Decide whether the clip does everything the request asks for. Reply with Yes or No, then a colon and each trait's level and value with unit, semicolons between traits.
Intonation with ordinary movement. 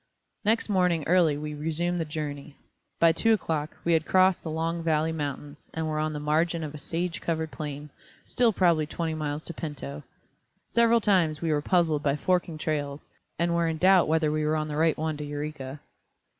No: narrow, 2.2 semitones